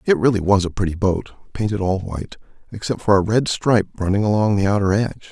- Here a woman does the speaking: No, male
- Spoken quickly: Yes, fast, 215 wpm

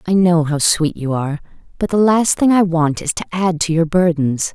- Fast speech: Yes, fast, 240 wpm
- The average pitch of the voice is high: No, medium, 170 Hz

